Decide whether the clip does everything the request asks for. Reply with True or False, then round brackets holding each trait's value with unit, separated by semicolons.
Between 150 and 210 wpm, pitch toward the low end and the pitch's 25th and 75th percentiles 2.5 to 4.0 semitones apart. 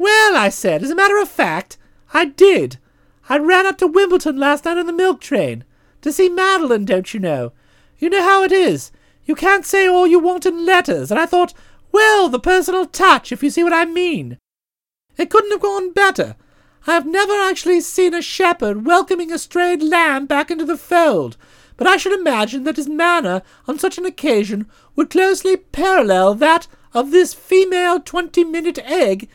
False (190 wpm; 350 Hz; 3.7 semitones)